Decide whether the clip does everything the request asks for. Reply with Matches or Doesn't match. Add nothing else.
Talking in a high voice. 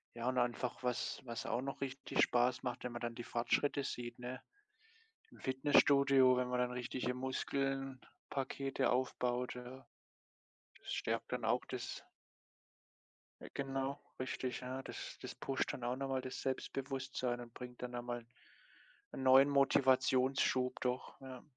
Doesn't match